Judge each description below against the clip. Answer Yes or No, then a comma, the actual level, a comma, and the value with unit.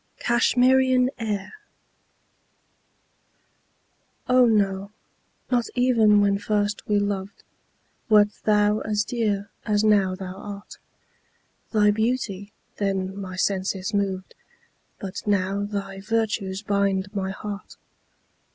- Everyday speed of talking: No, slow, 100 wpm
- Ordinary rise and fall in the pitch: No, narrow, 1.8 semitones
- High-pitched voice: Yes, high, 205 Hz